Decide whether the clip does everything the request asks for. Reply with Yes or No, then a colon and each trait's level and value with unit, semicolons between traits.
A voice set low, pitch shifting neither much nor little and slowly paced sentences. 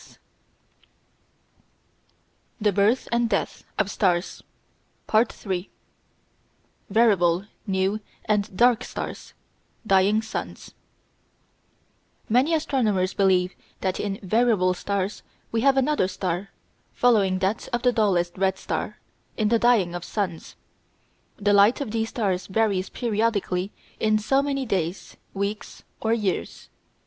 No: high, 205 Hz; average, 3.4 semitones; slow, 115 wpm